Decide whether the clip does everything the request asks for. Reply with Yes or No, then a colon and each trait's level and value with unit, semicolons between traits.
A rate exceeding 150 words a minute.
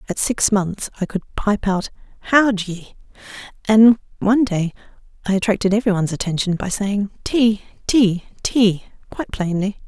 No: average, 145 wpm